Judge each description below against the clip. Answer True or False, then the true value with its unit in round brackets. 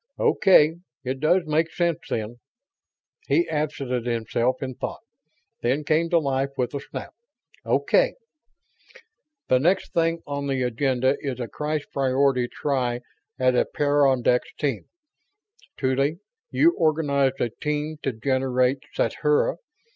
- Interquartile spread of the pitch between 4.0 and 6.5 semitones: False (3.1 semitones)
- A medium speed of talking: False (125 wpm)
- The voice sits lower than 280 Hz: True (140 Hz)